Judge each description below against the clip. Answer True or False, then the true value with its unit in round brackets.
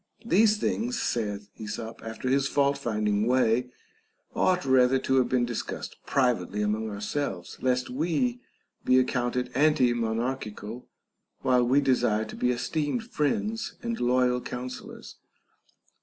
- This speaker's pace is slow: True (125 wpm)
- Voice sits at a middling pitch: False (125 Hz)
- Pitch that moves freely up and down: False (3.8 semitones)